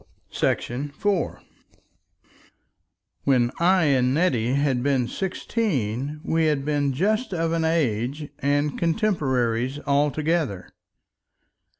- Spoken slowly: Yes, slow, 95 wpm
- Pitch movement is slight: No, average, 4.4 semitones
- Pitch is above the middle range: No, medium, 145 Hz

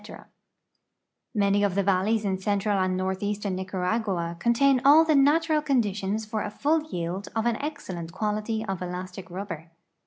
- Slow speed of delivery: No, average, 150 wpm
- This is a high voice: Yes, high, 205 Hz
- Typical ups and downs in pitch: Yes, average, 3.4 semitones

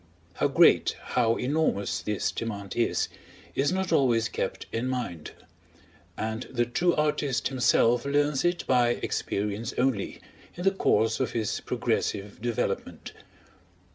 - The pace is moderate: No, slow, 130 wpm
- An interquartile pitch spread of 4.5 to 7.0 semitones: No, average, 4.1 semitones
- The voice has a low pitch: Yes, low, 120 Hz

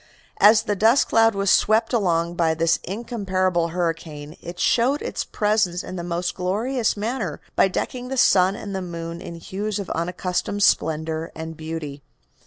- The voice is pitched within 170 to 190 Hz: Yes, medium, 185 Hz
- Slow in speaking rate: No, average, 165 wpm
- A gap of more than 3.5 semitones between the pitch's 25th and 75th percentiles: Yes, average, 4.2 semitones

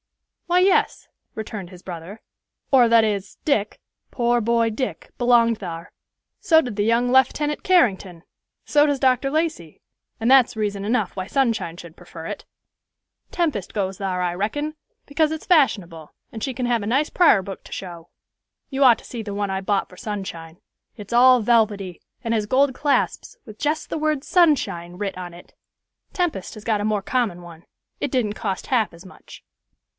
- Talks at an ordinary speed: Yes, average, 180 wpm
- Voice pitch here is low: No, high, 220 Hz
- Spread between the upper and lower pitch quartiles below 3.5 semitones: No, wide, 5.6 semitones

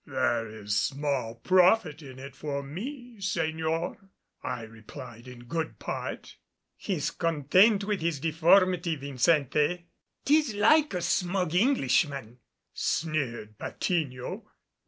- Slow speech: Yes, slow, 110 wpm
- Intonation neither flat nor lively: No, wide, 5.9 semitones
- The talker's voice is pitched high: No, medium, 160 Hz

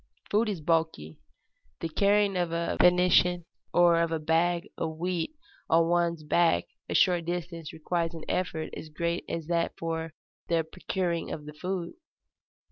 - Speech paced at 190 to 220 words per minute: No, average, 155 wpm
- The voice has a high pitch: No, medium, 170 Hz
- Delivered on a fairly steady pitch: Yes, narrow, 1.6 semitones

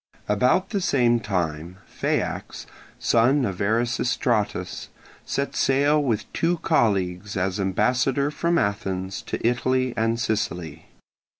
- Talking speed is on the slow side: Yes, slow, 110 wpm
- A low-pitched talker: Yes, low, 115 Hz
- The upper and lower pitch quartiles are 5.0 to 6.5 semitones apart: Yes, average, 5.3 semitones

